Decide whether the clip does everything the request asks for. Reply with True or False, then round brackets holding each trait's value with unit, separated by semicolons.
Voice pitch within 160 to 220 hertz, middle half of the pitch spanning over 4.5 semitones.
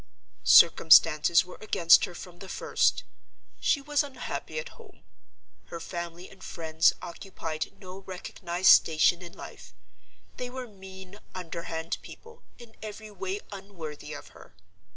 False (185 Hz; 3.7 semitones)